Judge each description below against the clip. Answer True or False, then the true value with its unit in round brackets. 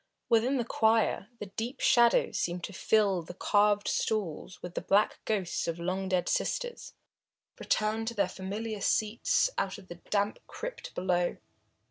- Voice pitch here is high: True (205 Hz)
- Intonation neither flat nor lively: True (3.2 semitones)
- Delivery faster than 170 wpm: False (155 wpm)